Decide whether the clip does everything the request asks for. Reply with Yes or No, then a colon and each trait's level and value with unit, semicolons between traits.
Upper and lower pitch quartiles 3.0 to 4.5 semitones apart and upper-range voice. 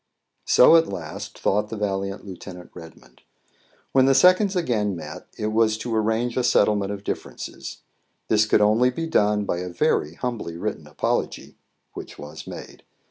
No: average, 4.0 semitones; low, 105 Hz